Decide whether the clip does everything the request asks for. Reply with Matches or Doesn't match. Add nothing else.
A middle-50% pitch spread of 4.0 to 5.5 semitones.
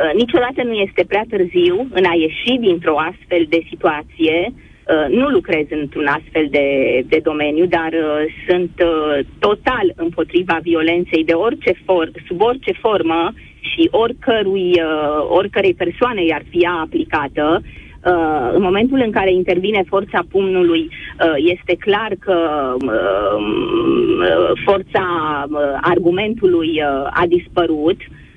Matches